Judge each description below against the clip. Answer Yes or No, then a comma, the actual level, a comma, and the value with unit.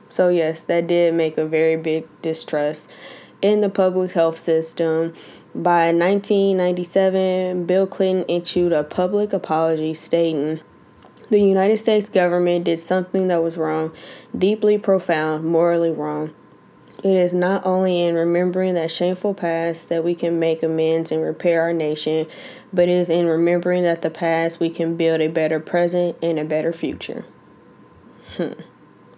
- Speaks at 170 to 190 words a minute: No, average, 150 wpm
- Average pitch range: No, narrow, 2.3 semitones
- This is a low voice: No, medium, 170 Hz